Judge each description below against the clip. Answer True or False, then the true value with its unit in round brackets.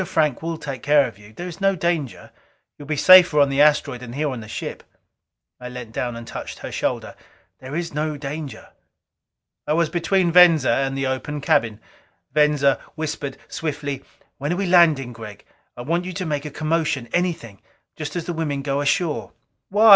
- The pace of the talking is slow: False (190 wpm)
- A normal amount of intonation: True (3.8 semitones)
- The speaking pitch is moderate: True (150 Hz)